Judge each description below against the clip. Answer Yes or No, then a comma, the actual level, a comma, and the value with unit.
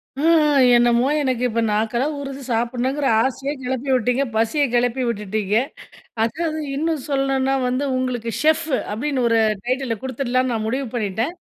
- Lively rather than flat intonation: No, average, 2.9 semitones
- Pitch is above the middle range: Yes, very high, 255 Hz